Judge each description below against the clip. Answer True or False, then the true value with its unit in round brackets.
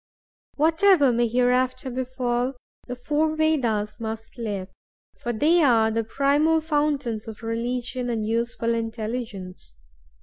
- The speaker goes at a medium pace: False (115 wpm)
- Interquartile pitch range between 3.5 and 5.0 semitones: True (3.8 semitones)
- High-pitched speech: True (245 Hz)